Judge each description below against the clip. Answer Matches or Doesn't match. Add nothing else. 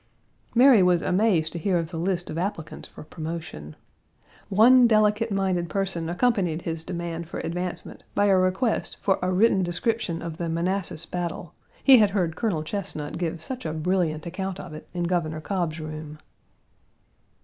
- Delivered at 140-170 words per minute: Matches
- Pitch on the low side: Doesn't match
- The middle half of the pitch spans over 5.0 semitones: Doesn't match